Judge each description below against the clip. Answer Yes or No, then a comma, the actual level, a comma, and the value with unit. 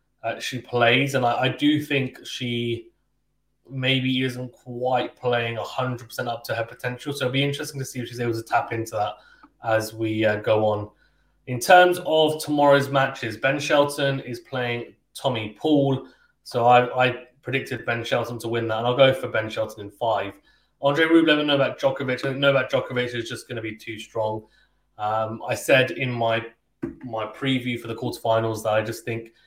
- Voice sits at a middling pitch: No, low, 125 Hz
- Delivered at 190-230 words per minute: Yes, average, 200 wpm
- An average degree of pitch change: Yes, average, 3.0 semitones